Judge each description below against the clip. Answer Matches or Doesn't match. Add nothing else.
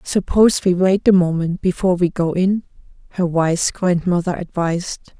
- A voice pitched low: Doesn't match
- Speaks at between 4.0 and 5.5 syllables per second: Matches